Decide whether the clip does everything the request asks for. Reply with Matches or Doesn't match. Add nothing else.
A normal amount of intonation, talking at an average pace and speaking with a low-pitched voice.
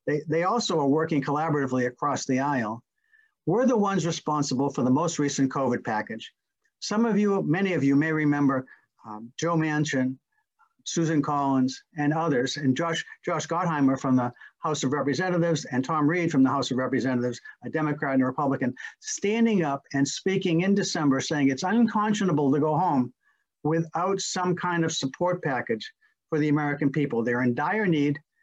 Doesn't match